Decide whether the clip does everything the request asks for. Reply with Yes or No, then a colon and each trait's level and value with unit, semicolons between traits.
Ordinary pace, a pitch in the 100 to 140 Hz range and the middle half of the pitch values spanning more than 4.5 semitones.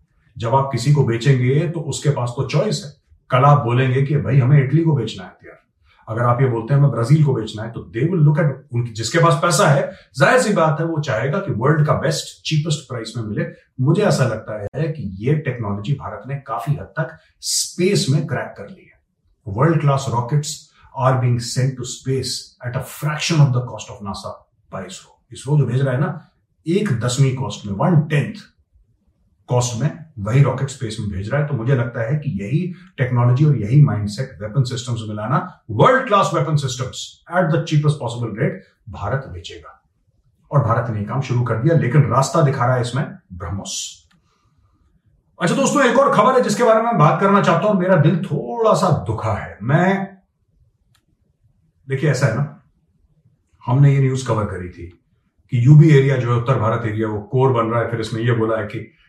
No: fast, 200 wpm; low, 135 Hz; average, 4.9 semitones